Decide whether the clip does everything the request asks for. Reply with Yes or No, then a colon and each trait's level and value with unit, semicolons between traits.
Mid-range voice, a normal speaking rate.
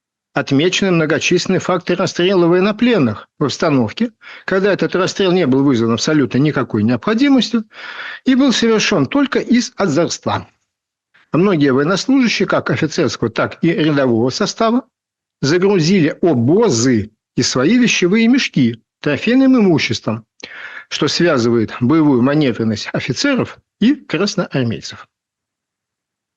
No: medium, 175 Hz; slow, 100 wpm